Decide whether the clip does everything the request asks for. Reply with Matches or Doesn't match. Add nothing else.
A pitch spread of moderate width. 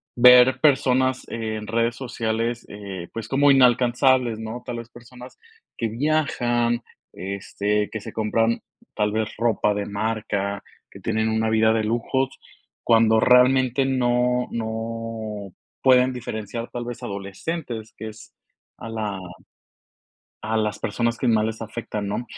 Doesn't match